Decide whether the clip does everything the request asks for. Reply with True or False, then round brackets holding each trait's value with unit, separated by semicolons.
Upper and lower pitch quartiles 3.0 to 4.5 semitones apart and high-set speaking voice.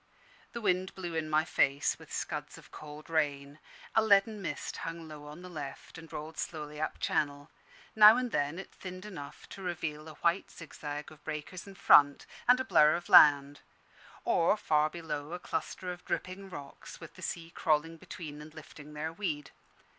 False (3.3 semitones; 160 Hz)